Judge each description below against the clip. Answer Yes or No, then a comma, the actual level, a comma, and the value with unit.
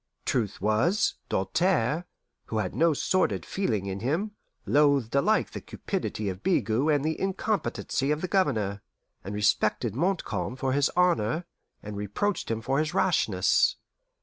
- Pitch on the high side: No, low, 135 Hz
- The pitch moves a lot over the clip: Yes, wide, 8.2 semitones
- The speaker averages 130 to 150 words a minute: Yes, average, 145 wpm